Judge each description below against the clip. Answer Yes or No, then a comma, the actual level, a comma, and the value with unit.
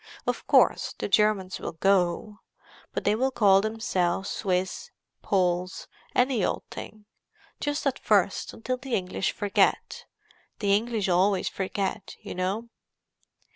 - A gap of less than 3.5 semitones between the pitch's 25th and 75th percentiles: Yes, average, 3.1 semitones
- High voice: Yes, high, 200 Hz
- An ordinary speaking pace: No, slow, 125 wpm